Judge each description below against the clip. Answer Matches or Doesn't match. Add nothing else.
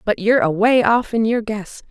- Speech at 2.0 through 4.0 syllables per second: Doesn't match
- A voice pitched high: Matches